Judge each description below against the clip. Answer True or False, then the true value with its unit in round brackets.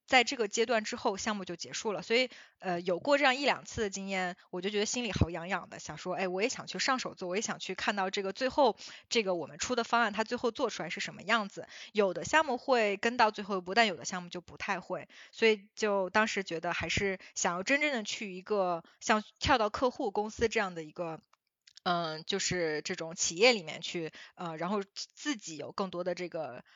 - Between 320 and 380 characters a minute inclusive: True (325 characters per minute)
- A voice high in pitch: True (200 Hz)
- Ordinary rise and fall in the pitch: True (4.5 semitones)